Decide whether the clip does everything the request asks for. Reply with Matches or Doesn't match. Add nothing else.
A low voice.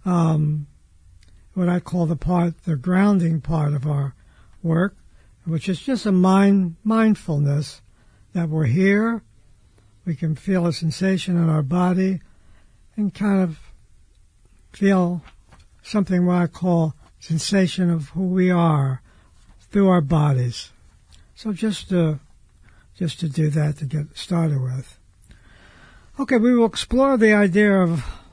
Doesn't match